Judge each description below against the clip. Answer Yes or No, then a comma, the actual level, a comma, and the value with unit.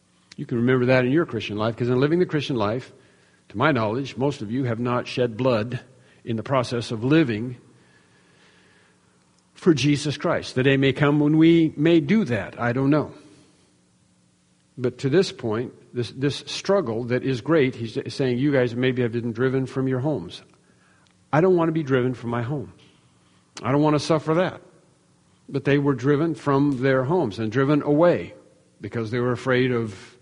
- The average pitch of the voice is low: Yes, low, 130 Hz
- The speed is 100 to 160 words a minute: No, average, 190 wpm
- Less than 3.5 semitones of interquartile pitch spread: No, average, 3.8 semitones